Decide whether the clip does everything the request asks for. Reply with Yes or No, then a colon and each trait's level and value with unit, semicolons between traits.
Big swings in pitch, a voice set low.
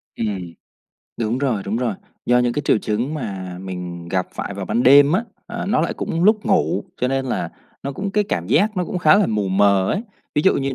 Yes: wide, 8.8 semitones; low, 125 Hz